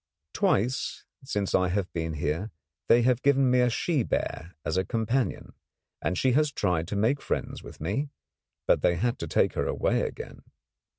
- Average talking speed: Yes, average, 180 wpm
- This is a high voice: No, low, 110 Hz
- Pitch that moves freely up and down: Yes, wide, 6.2 semitones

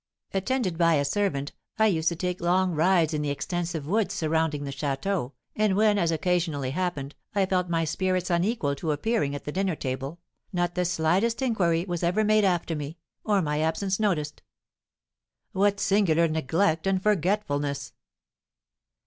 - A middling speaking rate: Yes, average, 160 wpm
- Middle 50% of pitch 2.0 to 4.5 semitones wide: Yes, average, 4.1 semitones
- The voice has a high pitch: No, medium, 175 Hz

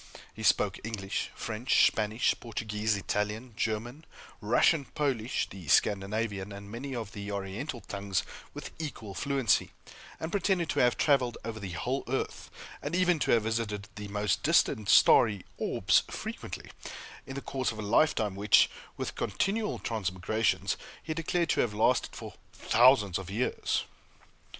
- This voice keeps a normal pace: Yes, average, 145 wpm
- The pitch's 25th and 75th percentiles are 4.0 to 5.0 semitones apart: Yes, average, 4.5 semitones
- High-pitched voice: No, low, 110 Hz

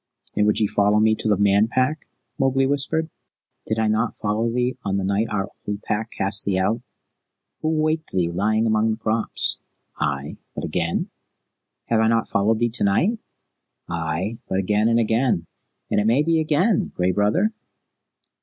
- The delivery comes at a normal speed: Yes, average, 175 wpm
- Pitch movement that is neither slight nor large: Yes, average, 3.5 semitones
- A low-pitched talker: Yes, low, 110 Hz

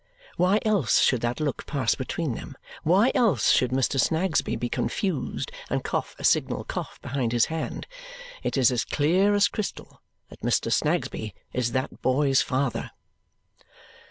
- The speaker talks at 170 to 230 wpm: No, average, 155 wpm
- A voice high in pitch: No, medium, 140 Hz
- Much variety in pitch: Yes, wide, 6.3 semitones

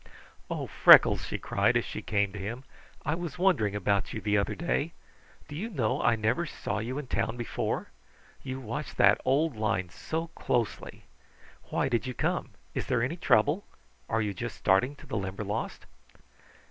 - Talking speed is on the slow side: No, average, 175 wpm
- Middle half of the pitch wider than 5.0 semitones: Yes, wide, 5.6 semitones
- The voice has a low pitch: Yes, low, 120 Hz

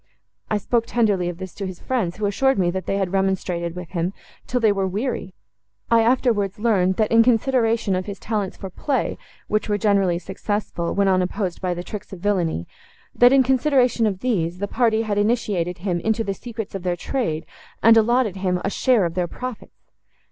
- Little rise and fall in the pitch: No, average, 3.8 semitones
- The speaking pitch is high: Yes, high, 200 Hz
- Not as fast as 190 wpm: No, average, 195 wpm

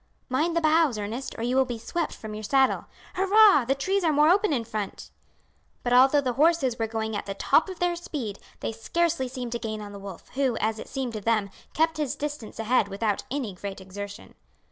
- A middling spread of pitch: No, wide, 5.9 semitones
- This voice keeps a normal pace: No, fast, 220 wpm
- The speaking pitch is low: No, very high, 250 Hz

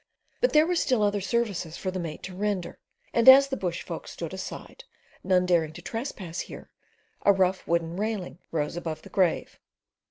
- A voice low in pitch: No, high, 190 Hz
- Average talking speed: Yes, average, 185 wpm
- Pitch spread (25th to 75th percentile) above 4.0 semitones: Yes, average, 4.5 semitones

